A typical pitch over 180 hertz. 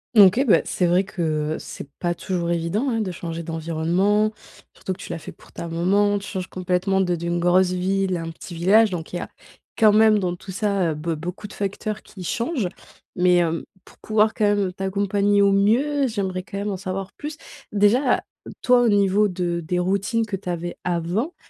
Yes: high, 190 Hz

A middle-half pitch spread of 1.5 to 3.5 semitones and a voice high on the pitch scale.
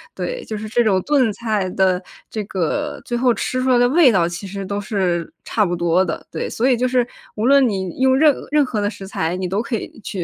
No: average, 5.1 semitones; high, 215 Hz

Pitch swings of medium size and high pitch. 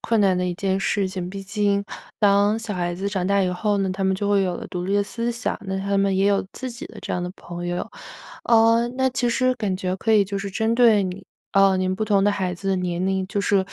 No: narrow, 2.0 semitones; high, 195 Hz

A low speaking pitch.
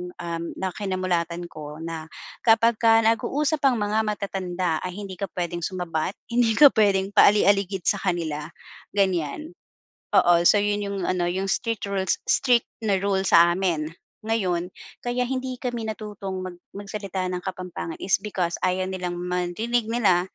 No: high, 190 Hz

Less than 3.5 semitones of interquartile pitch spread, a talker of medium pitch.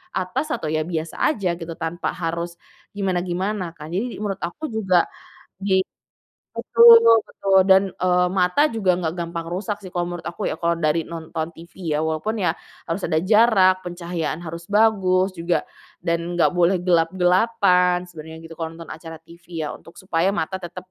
Yes: narrow, 2.4 semitones; medium, 180 Hz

